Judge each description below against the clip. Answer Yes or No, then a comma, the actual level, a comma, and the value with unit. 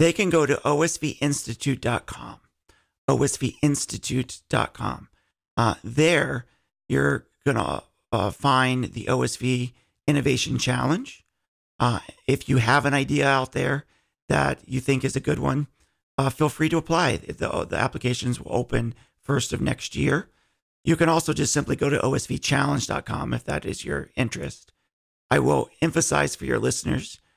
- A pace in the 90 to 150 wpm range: Yes, average, 140 wpm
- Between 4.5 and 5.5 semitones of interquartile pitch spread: No, average, 3.3 semitones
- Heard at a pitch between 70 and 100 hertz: No, low, 135 Hz